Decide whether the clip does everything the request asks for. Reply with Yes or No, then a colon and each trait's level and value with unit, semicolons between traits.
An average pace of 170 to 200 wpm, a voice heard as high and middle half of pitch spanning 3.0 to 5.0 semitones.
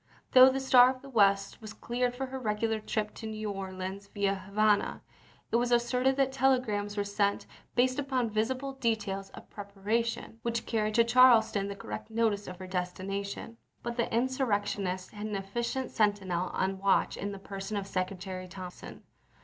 Yes: average, 180 wpm; high, 215 Hz; average, 3.4 semitones